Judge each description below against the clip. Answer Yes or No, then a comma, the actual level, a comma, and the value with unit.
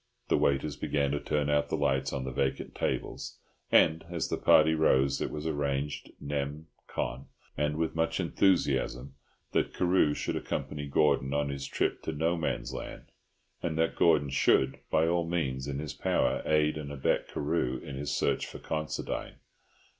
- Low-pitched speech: Yes, very low, 75 Hz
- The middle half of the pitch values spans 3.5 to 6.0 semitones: No, narrow, 2.4 semitones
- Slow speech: No, average, 170 wpm